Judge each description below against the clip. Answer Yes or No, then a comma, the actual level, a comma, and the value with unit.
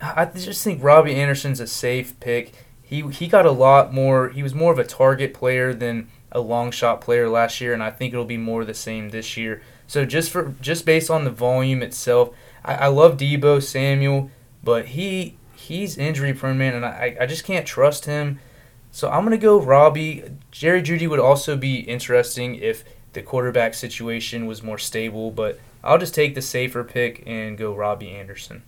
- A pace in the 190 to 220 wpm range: Yes, average, 200 wpm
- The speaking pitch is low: Yes, low, 130 Hz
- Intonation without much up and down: No, average, 3.6 semitones